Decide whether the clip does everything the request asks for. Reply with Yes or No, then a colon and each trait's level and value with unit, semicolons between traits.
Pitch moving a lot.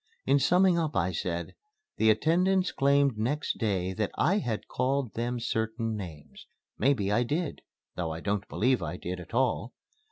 Yes: wide, 6.0 semitones